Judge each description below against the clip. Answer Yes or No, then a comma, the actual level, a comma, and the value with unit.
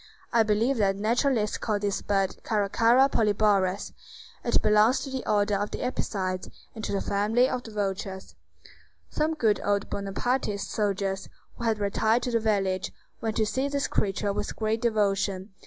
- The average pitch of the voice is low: No, high, 210 Hz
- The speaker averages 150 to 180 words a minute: Yes, average, 165 wpm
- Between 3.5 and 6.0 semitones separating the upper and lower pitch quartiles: No, narrow, 2.5 semitones